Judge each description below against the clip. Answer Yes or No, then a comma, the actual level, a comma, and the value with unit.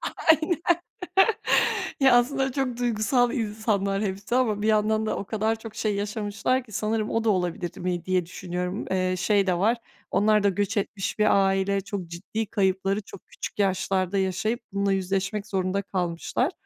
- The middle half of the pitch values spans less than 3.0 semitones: Yes, narrow, 2.5 semitones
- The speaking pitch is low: No, high, 205 Hz